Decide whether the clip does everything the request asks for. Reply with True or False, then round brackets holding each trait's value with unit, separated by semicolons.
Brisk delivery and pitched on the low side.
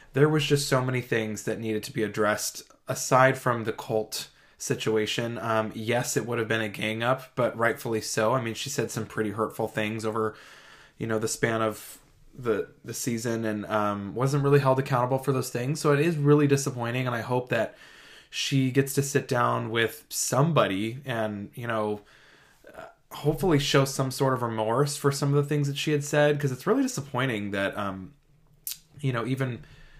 False (195 wpm; 125 Hz)